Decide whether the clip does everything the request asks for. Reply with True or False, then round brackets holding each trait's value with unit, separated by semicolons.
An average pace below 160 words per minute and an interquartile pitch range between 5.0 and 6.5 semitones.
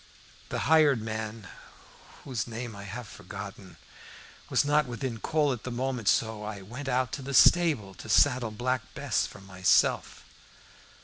False (150 wpm; 4.0 semitones)